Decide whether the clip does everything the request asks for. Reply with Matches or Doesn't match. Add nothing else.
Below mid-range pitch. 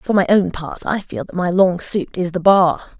Doesn't match